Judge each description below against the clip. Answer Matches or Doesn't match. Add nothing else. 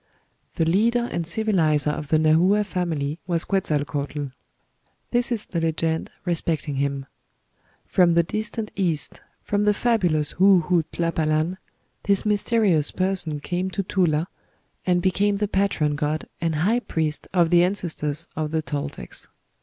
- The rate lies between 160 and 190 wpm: Doesn't match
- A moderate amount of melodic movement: Matches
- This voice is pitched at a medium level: Matches